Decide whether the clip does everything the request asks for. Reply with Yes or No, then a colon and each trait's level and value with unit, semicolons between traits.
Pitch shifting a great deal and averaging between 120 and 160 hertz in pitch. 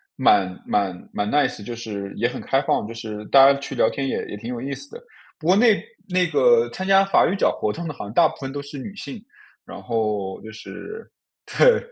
Yes: wide, 8.8 semitones; low, 135 Hz